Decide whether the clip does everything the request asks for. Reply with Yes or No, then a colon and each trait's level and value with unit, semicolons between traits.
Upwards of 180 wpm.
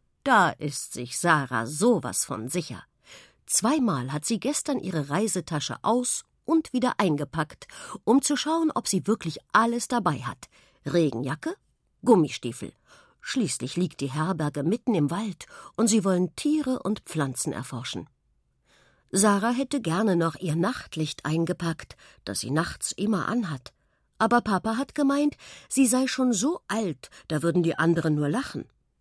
No: average, 145 wpm